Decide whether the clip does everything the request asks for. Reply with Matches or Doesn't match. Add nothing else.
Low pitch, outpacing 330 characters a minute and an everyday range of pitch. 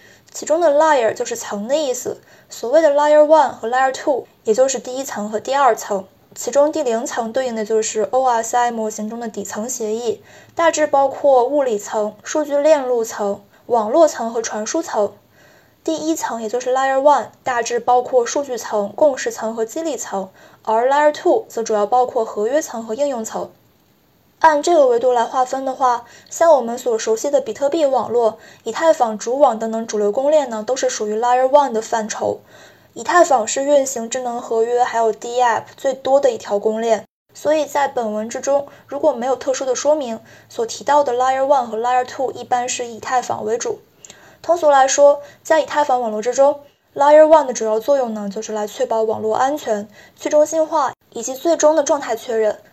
Doesn't match